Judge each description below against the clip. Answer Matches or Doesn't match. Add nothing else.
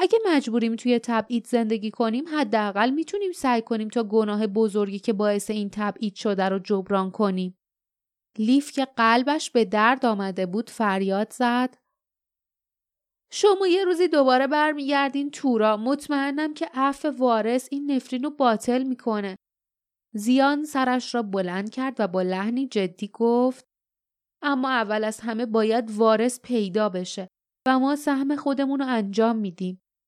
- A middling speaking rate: Matches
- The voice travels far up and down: Doesn't match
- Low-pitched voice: Doesn't match